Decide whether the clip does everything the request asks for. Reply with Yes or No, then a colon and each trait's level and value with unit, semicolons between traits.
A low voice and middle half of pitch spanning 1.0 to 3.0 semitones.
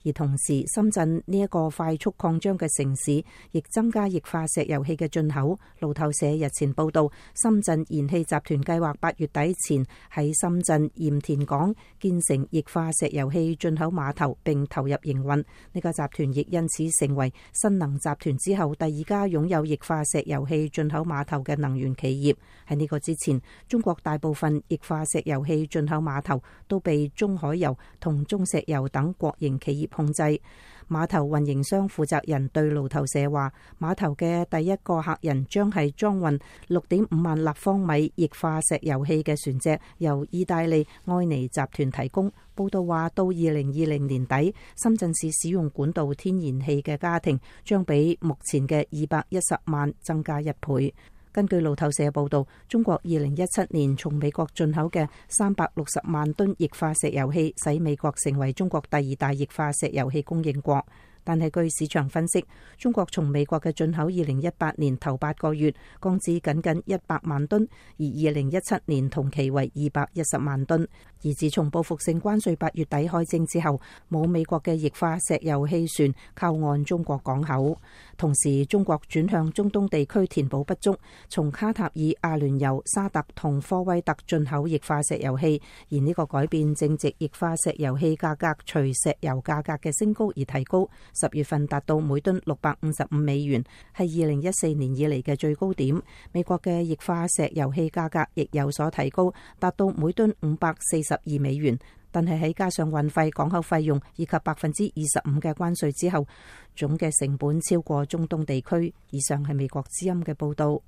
No: medium, 155 Hz; narrow, 2.6 semitones